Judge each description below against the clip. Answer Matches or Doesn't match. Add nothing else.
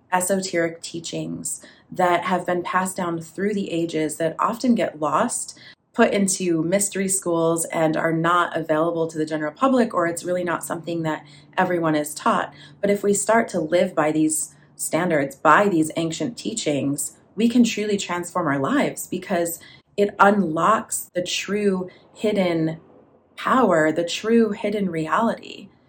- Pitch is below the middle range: Doesn't match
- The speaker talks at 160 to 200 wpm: Doesn't match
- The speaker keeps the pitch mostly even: Doesn't match